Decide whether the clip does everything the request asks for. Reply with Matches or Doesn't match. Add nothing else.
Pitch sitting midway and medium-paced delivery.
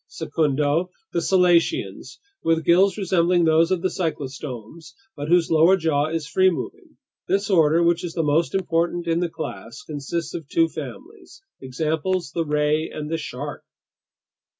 Matches